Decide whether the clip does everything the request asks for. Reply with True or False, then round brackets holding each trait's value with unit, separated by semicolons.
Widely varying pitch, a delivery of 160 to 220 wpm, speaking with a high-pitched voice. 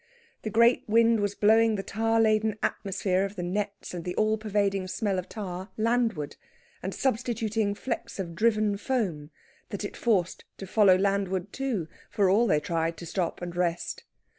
False (3.2 semitones; 170 wpm; 200 Hz)